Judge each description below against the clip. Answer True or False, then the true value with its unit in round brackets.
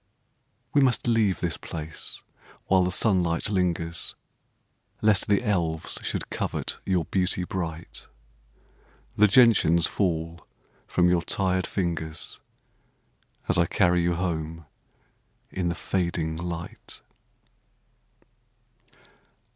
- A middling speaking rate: False (100 wpm)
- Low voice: True (90 Hz)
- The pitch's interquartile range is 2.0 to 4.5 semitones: True (2.4 semitones)